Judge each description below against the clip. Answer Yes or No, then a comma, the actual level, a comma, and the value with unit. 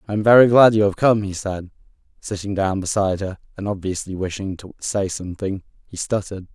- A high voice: No, low, 100 Hz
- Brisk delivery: No, average, 195 wpm